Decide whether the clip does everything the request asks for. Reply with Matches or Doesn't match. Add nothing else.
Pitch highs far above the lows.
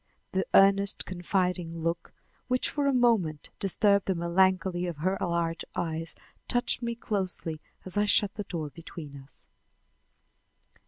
Doesn't match